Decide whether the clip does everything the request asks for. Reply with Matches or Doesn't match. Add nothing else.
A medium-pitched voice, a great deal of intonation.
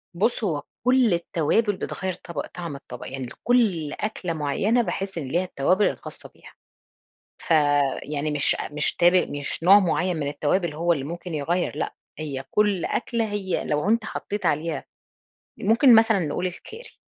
Matches